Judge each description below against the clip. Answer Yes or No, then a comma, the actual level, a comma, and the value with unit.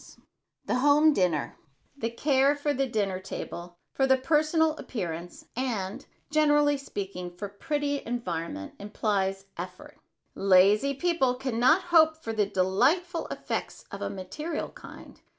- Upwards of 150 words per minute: No, slow, 135 wpm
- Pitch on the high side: Yes, high, 245 Hz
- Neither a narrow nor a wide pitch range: No, wide, 7.3 semitones